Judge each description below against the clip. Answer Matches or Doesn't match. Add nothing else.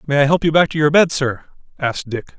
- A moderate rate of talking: Doesn't match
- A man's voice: Matches